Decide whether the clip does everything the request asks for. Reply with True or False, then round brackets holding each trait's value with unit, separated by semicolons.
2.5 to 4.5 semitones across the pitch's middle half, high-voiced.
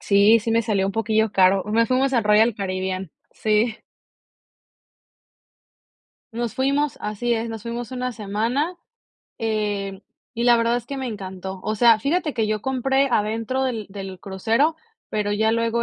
True (2.8 semitones; 225 Hz)